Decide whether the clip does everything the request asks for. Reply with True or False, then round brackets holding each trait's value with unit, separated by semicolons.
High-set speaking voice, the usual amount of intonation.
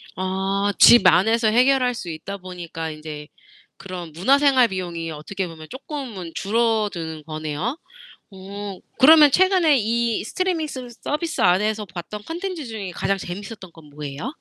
False (200 Hz; 6.4 semitones)